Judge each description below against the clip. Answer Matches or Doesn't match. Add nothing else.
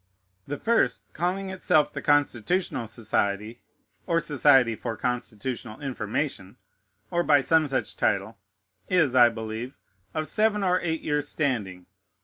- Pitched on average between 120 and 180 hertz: Matches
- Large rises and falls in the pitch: Matches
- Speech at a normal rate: Doesn't match